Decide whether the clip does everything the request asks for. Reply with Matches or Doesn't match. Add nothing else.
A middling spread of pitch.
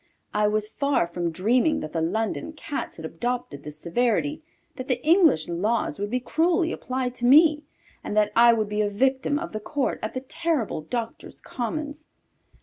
Doesn't match